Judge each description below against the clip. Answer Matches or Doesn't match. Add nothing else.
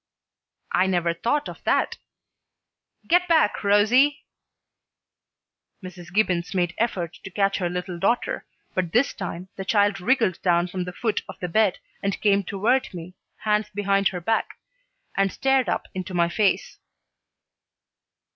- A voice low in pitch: Doesn't match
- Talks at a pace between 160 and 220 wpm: Doesn't match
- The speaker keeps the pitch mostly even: Doesn't match